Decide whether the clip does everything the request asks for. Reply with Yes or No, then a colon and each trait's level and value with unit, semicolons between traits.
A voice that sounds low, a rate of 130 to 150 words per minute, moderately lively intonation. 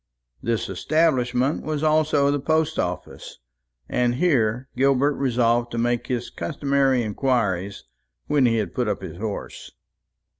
Yes: low, 125 Hz; slow, 135 wpm; average, 3.7 semitones